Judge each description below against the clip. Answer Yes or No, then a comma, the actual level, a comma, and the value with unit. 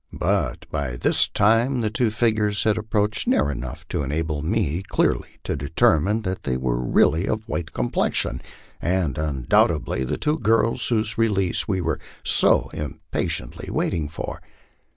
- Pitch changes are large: Yes, wide, 6.9 semitones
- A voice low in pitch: Yes, very low, 95 Hz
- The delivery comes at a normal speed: Yes, average, 150 wpm